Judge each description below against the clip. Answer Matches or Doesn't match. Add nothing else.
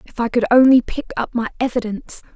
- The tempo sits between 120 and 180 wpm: Doesn't match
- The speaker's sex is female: Matches